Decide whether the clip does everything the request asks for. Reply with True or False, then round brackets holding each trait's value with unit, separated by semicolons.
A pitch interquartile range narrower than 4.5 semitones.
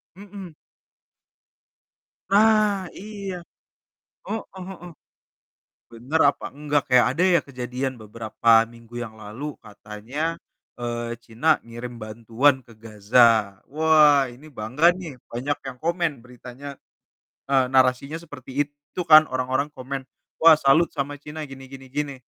False (4.8 semitones)